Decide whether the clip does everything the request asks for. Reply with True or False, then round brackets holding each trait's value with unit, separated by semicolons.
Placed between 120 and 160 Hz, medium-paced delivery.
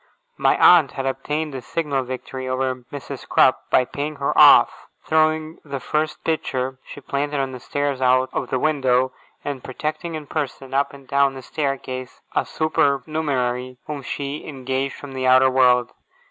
True (135 Hz; 160 wpm)